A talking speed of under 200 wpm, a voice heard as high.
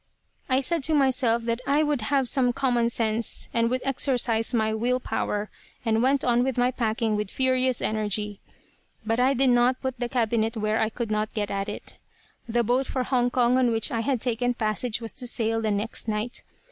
No: fast, 205 wpm; high, 240 Hz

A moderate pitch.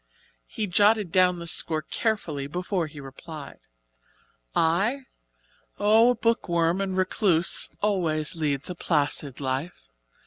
Yes: medium, 170 Hz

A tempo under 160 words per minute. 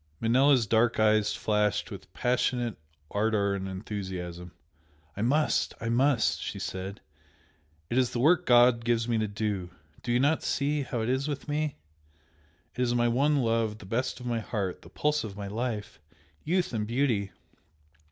No: average, 170 wpm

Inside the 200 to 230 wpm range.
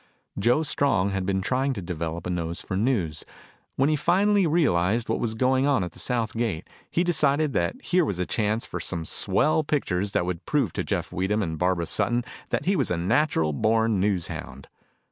Yes: fast, 205 wpm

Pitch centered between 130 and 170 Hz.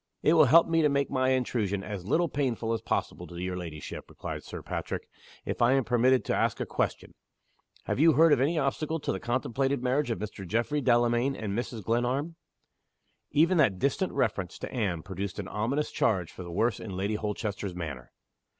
No: low, 120 Hz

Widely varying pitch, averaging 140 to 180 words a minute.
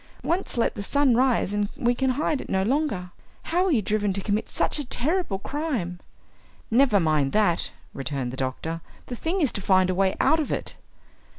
No: wide, 7.2 semitones; average, 200 wpm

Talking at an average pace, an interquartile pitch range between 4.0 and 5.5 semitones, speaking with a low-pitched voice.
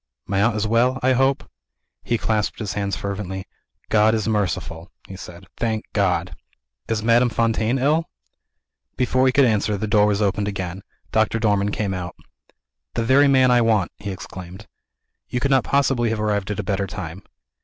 No: average, 175 wpm; average, 3.3 semitones; low, 105 Hz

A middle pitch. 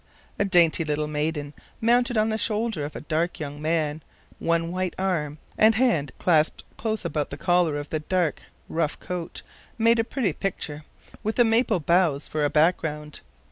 Yes: medium, 170 Hz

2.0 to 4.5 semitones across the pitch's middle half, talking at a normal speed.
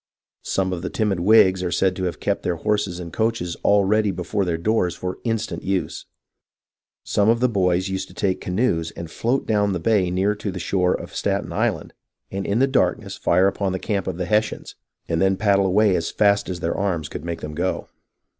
No: average, 2.8 semitones; fast, 215 wpm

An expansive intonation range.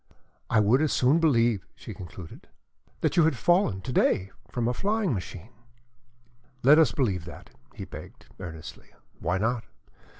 Yes: wide, 7.9 semitones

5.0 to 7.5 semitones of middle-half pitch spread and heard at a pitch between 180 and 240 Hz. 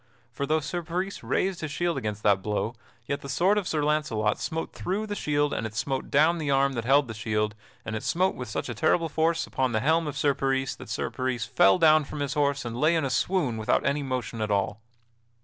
No: average, 5.3 semitones; medium, 140 Hz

